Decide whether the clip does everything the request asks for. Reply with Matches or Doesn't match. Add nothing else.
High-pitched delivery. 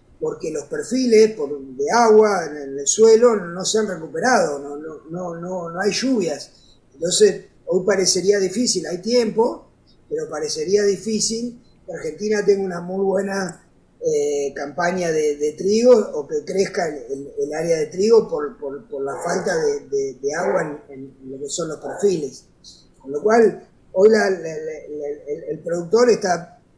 Matches